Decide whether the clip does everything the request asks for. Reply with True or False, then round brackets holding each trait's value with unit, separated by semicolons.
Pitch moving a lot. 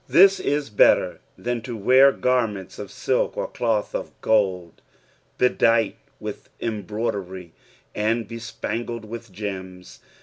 False (3.1 semitones)